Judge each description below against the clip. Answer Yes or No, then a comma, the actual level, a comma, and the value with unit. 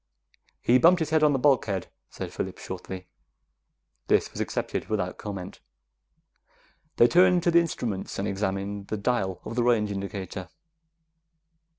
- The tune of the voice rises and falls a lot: Yes, wide, 6.8 semitones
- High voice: No, low, 105 Hz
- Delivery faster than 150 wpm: No, average, 145 wpm